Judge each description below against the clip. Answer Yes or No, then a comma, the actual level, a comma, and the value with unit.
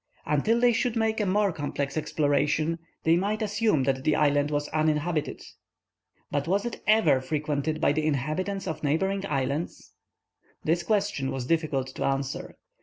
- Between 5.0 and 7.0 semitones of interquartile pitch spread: Yes, wide, 5.4 semitones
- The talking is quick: No, average, 155 wpm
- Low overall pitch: No, medium, 155 Hz